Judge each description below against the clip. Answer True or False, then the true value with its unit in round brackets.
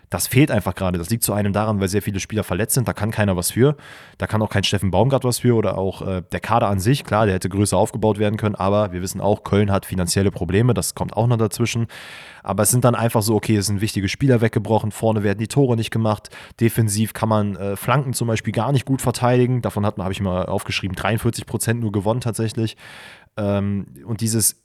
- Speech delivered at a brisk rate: True (240 wpm)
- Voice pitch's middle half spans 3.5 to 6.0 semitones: False (2.7 semitones)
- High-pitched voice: False (110 Hz)